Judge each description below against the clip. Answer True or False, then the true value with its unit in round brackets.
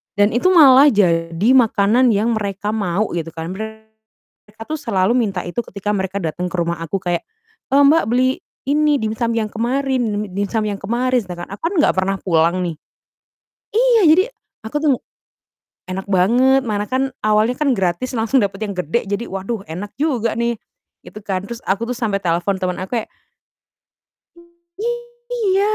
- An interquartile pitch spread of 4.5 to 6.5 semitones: True (4.8 semitones)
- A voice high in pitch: True (215 Hz)